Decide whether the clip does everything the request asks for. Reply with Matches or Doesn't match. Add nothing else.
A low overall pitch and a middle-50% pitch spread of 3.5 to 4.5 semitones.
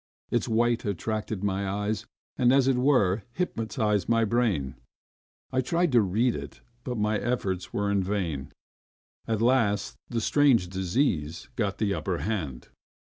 Matches